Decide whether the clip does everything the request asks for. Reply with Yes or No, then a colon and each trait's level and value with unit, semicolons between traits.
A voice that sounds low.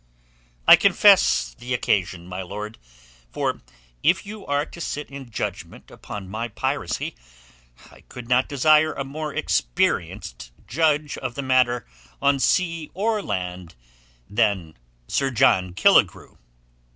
Yes: low, 125 Hz